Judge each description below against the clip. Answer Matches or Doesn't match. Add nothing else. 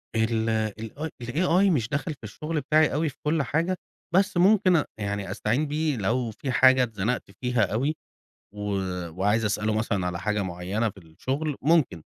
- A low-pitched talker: Matches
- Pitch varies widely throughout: Matches